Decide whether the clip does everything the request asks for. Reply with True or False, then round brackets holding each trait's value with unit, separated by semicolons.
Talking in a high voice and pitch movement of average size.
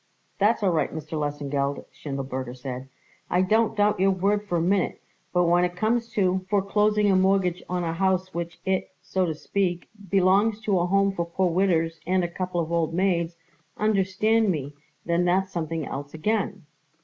False (180 Hz; 3.1 semitones)